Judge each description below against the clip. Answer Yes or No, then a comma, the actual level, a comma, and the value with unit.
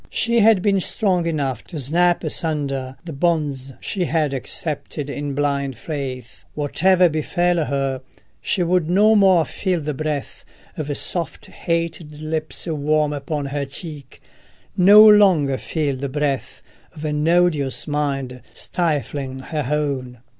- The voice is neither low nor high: Yes, medium, 150 Hz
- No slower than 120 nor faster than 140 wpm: Yes, slow, 135 wpm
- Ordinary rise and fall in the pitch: Yes, average, 3.8 semitones